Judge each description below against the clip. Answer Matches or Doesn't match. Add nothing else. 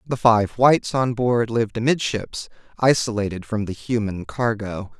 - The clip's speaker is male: Matches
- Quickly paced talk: Doesn't match